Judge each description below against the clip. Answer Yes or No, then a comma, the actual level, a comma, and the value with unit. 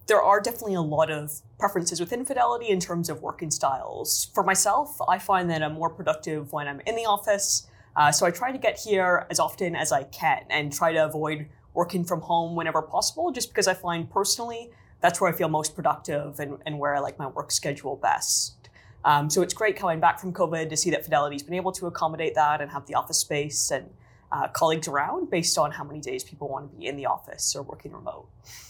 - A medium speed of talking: No, fast, 230 wpm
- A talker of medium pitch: Yes, medium, 170 Hz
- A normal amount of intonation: Yes, average, 4.2 semitones